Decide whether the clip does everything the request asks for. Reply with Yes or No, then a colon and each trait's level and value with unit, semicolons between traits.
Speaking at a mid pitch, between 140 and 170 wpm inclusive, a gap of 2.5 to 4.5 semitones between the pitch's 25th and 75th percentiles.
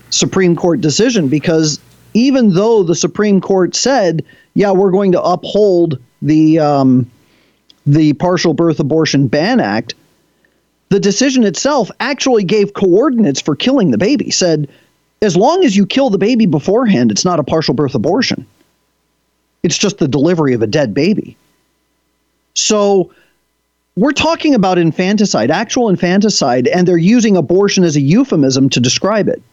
No: medium, 180 Hz; average, 150 wpm; average, 5.1 semitones